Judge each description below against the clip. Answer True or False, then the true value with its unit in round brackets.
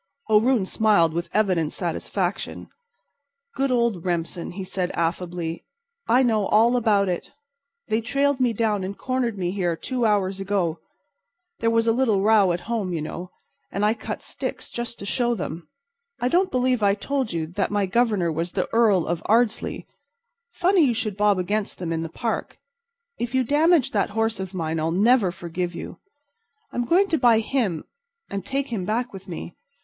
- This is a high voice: True (210 Hz)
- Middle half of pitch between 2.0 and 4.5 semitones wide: False (5.0 semitones)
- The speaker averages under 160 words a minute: False (180 wpm)